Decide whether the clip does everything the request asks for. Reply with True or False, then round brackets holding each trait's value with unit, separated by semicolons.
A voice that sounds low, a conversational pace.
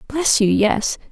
False (240 Hz; 160 wpm)